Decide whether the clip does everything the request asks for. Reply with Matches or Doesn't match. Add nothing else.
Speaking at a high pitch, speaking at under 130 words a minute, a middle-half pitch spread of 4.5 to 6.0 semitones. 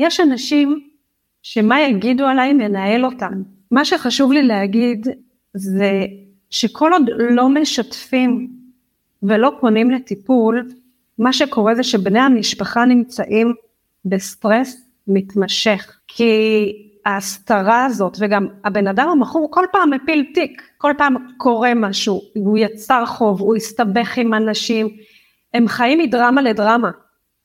Doesn't match